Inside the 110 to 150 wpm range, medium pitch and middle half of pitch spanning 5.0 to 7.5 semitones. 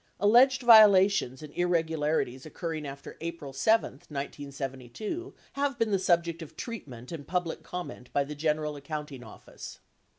Yes: average, 140 wpm; medium, 160 Hz; wide, 5.5 semitones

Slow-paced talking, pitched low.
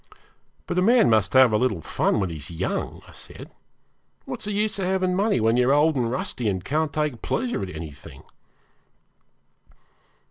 No: average, 180 wpm; low, 130 Hz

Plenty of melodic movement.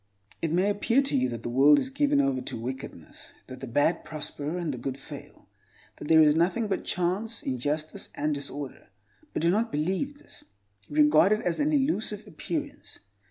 Yes: wide, 7.8 semitones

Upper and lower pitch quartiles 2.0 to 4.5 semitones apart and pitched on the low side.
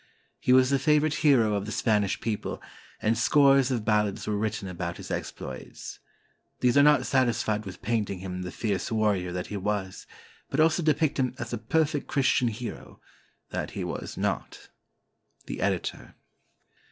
No: average, 5.0 semitones; low, 110 Hz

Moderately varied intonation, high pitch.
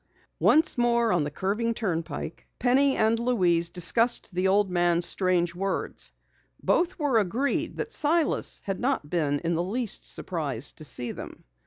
No: wide, 5.8 semitones; high, 195 Hz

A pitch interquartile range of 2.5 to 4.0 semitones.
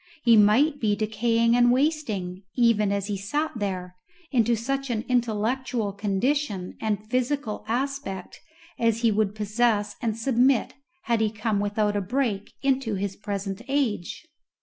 Yes: average, 3.4 semitones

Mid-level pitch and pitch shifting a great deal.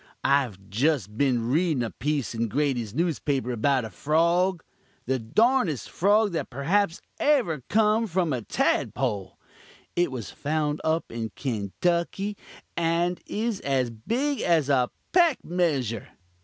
Yes: medium, 150 Hz; wide, 6.4 semitones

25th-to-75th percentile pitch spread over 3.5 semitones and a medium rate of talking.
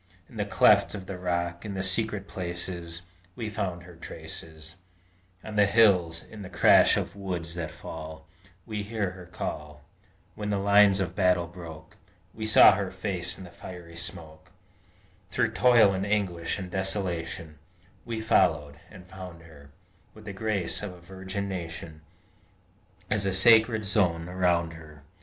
No: average, 3.2 semitones; average, 155 wpm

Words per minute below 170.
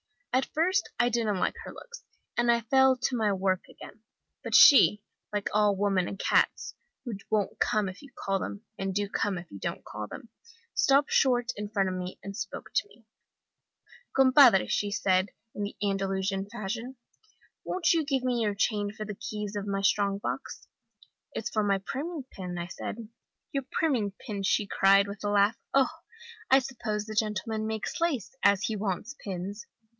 No: average, 185 wpm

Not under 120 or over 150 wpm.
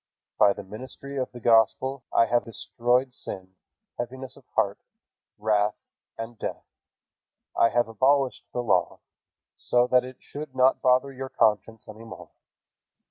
Yes: average, 140 wpm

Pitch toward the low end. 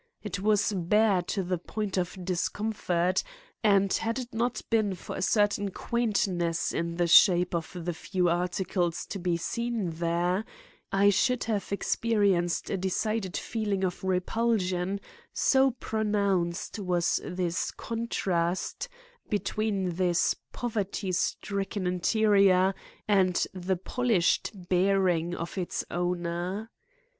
No: high, 190 Hz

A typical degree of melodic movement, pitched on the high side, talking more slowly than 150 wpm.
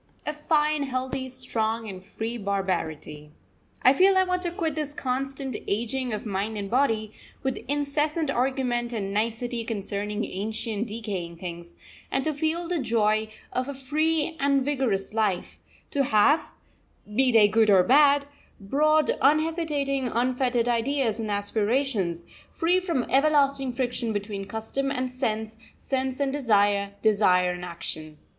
Yes: average, 5.0 semitones; high, 245 Hz; average, 140 wpm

